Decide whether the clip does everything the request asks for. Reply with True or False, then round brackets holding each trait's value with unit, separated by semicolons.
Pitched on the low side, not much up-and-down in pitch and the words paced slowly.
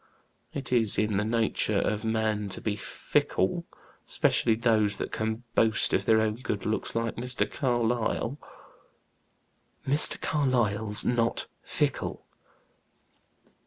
True (110 Hz; 2.0 semitones; 120 wpm)